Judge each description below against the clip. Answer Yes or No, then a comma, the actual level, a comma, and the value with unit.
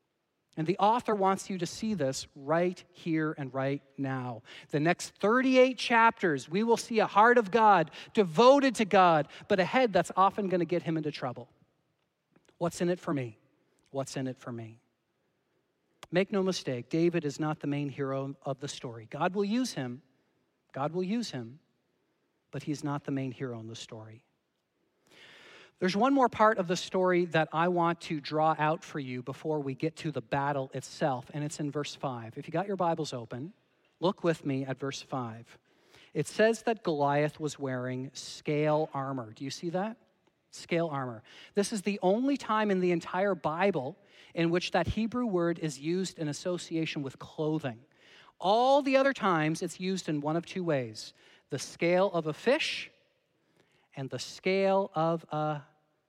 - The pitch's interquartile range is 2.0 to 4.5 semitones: No, average, 5.2 semitones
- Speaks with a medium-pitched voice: Yes, medium, 160 Hz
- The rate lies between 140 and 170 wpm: No, average, 185 wpm